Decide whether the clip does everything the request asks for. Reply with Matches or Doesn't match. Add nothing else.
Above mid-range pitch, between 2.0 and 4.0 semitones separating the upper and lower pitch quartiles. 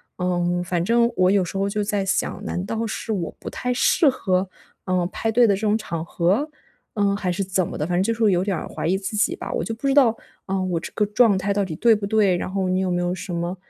Matches